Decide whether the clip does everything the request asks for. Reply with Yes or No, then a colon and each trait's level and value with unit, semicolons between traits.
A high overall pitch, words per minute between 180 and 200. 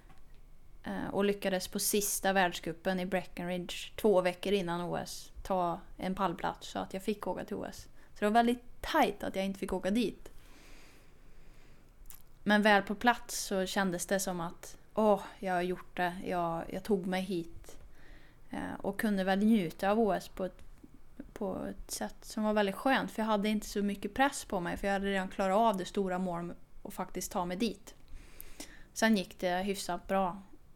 Yes: high, 195 Hz; average, 185 wpm